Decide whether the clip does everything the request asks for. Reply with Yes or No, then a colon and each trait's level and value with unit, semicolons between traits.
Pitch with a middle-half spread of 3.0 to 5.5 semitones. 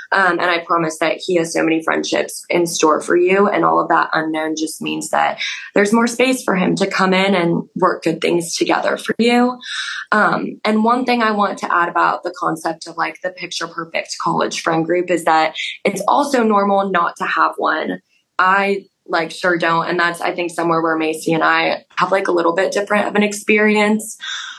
Yes: average, 3.8 semitones